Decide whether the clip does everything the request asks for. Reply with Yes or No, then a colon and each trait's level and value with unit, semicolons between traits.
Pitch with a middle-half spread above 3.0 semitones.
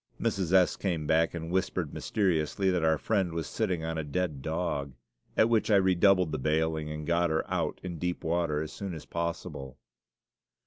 No: average, 2.7 semitones